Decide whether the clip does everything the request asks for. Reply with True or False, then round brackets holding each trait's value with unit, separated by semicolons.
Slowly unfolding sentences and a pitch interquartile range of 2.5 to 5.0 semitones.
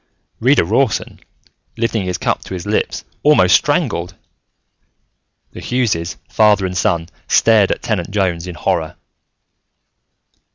True (120 wpm; 4.0 semitones)